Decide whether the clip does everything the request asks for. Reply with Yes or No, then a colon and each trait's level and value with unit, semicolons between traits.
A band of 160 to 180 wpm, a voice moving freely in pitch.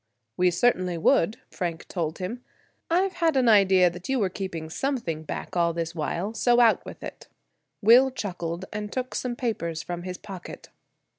Yes: average, 170 wpm; wide, 6.0 semitones